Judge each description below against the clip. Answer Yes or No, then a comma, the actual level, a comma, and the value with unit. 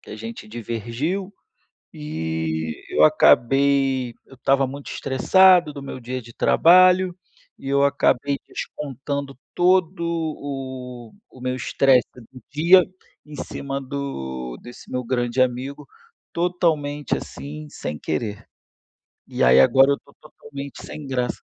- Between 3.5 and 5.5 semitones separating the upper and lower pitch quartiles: Yes, average, 3.8 semitones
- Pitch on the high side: No, low, 135 Hz